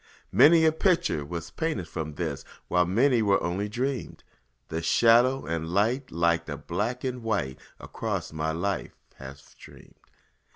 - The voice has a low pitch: Yes, low, 100 Hz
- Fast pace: No, average, 150 wpm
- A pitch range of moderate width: No, wide, 7.4 semitones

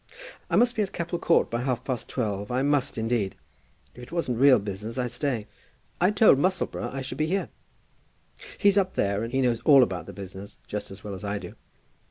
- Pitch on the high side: No, low, 125 Hz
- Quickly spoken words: Yes, fast, 215 wpm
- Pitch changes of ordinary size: No, wide, 6.8 semitones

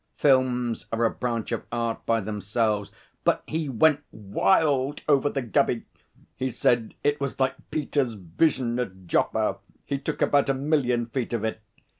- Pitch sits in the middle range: No, low, 125 Hz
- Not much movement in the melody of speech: No, average, 3.6 semitones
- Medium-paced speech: Yes, average, 160 wpm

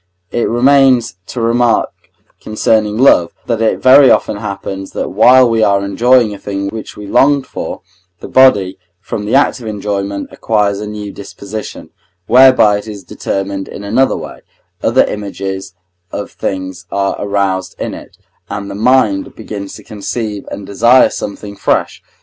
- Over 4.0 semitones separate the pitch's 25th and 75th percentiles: No, average, 3.0 semitones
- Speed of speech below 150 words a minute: No, average, 155 wpm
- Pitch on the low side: Yes, low, 105 Hz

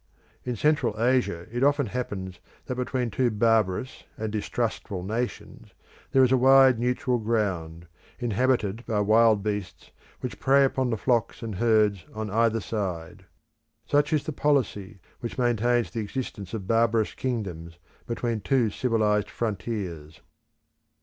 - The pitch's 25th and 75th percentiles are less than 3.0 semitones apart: No, average, 3.6 semitones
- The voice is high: No, low, 115 Hz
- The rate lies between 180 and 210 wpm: No, slow, 135 wpm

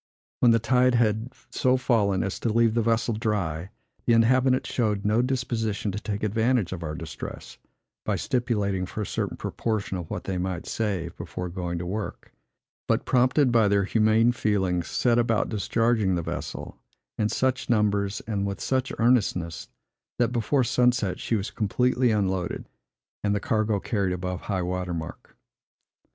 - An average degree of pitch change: Yes, average, 3.9 semitones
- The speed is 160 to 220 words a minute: Yes, average, 165 wpm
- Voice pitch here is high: No, low, 105 Hz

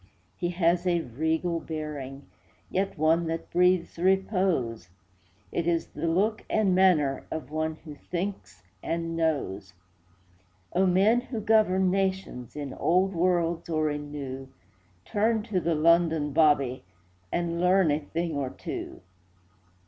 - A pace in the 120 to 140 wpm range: Yes, slow, 135 wpm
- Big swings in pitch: No, average, 3.8 semitones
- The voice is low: No, medium, 165 Hz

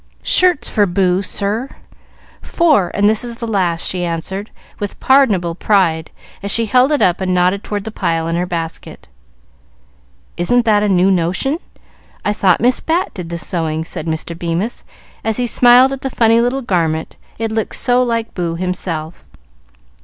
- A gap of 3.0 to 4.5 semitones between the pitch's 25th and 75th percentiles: No, average, 5.2 semitones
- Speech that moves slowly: No, average, 170 wpm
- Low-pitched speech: No, high, 200 Hz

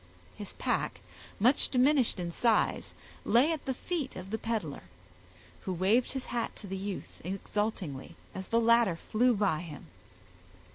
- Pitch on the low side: No, high, 215 Hz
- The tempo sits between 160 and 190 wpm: No, average, 150 wpm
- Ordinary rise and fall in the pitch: Yes, average, 4.6 semitones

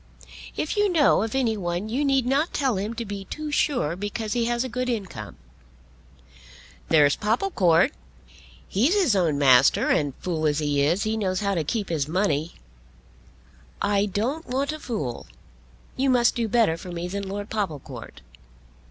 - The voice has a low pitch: No, high, 205 Hz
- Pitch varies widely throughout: Yes, wide, 6.5 semitones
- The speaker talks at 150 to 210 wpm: Yes, average, 170 wpm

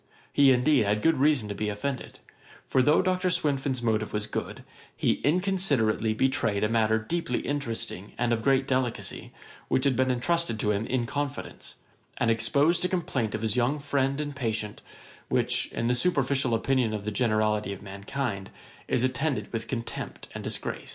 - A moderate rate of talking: Yes, average, 170 wpm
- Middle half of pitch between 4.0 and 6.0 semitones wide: Yes, average, 4.5 semitones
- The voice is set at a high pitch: No, low, 125 Hz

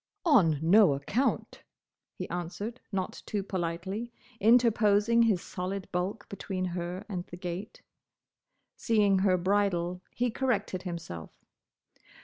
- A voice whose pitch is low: No, high, 195 Hz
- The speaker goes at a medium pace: No, slow, 115 wpm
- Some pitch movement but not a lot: Yes, average, 3.4 semitones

